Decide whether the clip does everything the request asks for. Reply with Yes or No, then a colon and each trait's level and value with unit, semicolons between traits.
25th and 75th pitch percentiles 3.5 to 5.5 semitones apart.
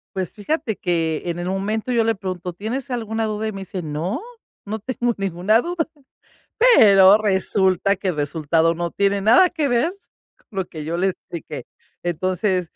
Yes: average, 4.1 semitones